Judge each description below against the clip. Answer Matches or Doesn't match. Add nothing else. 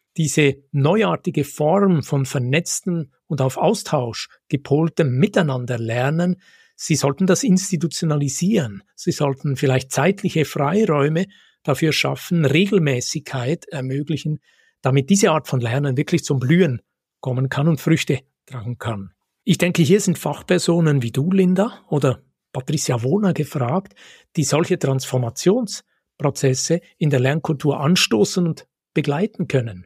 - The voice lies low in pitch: Doesn't match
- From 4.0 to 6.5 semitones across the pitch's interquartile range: Matches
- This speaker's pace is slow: Matches